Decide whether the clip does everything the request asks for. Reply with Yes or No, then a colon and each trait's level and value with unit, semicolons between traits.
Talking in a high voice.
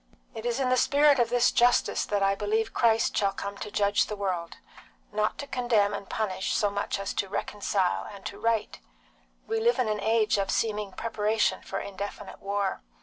Yes: high, 210 Hz